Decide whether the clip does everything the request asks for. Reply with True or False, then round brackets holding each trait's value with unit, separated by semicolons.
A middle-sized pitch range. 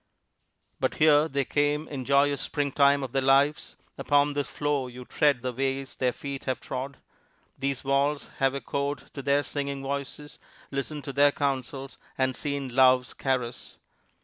False (1.4 semitones)